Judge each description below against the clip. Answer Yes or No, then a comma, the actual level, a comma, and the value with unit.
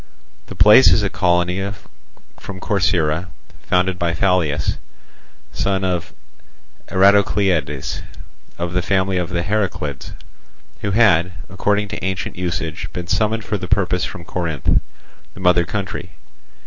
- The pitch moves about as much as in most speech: No, narrow, 2.3 semitones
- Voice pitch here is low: Yes, very low, 90 Hz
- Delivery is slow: Yes, slow, 125 wpm